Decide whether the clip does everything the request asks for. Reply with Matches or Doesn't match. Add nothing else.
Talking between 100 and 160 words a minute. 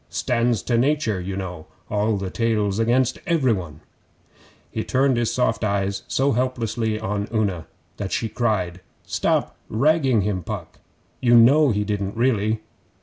Matches